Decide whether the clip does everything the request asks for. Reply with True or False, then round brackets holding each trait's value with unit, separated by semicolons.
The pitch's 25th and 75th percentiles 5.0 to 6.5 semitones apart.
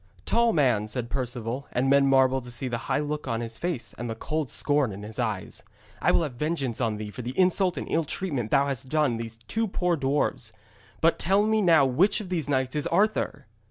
True (5.5 semitones)